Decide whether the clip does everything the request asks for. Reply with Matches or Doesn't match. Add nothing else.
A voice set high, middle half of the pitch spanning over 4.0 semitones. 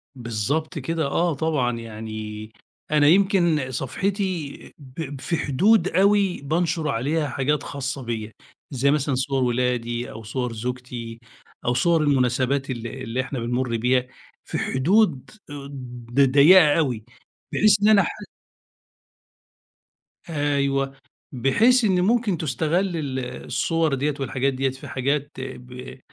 Doesn't match